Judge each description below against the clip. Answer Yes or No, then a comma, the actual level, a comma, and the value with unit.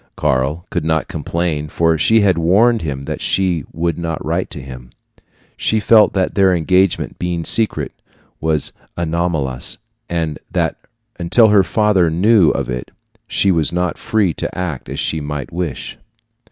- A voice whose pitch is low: Yes, very low, 85 Hz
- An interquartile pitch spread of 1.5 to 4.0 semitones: Yes, average, 3.7 semitones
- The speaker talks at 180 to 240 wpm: No, average, 155 wpm